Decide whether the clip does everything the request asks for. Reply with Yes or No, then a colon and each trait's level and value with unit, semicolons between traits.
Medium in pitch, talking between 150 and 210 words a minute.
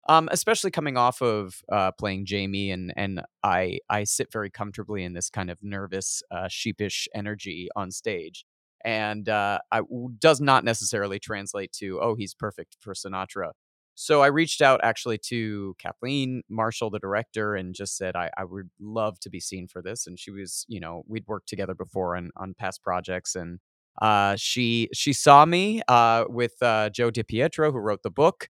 No: low, 105 Hz; average, 185 wpm